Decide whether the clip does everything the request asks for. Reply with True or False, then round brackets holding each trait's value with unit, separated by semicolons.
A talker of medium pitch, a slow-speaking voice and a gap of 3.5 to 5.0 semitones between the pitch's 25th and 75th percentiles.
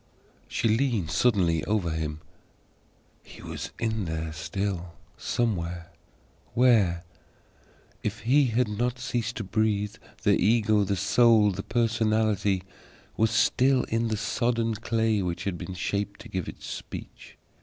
False (105 Hz; 130 wpm; 3.9 semitones)